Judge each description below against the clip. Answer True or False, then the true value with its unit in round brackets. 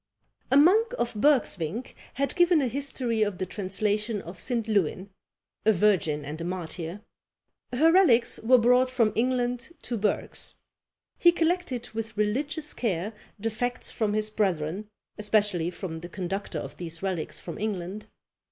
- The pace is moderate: True (150 wpm)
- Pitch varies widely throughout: False (5.0 semitones)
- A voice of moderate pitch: False (215 Hz)